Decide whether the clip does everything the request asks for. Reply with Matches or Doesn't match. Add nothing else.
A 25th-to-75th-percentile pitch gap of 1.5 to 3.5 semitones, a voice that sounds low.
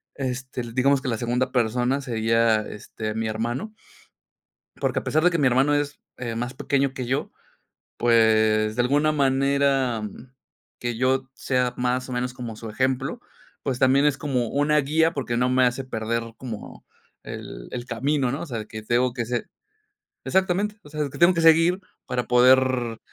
Matches